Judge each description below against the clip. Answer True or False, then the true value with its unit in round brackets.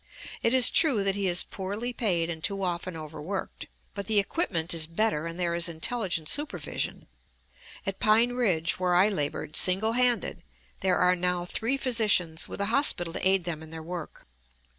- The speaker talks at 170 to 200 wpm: True (180 wpm)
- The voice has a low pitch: False (185 Hz)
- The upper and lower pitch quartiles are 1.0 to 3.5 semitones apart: False (4.5 semitones)